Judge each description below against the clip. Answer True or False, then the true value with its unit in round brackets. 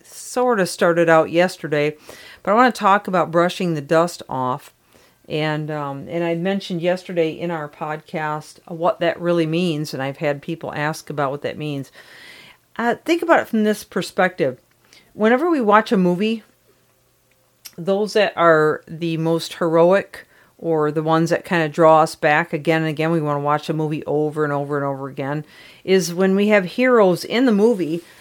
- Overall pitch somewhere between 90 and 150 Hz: False (165 Hz)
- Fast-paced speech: False (185 wpm)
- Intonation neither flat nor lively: True (4.0 semitones)